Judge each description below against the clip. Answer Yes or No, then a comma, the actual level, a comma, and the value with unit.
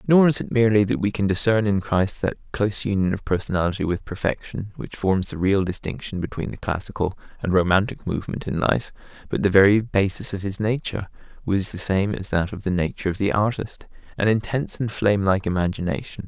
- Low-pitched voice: Yes, low, 100 Hz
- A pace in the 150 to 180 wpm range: No, average, 190 wpm